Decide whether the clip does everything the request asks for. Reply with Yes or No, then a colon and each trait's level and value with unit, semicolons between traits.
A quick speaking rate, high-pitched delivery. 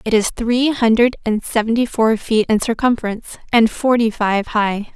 No: average, 170 wpm; high, 225 Hz